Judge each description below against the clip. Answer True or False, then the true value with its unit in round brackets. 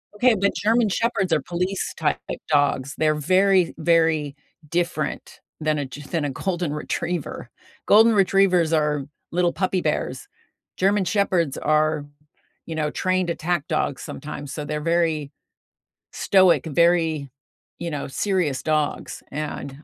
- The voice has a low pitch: False (165 Hz)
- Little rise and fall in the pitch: False (3.6 semitones)